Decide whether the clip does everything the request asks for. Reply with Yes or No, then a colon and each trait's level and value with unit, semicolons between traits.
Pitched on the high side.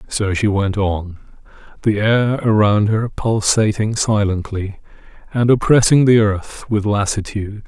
No: low, 105 Hz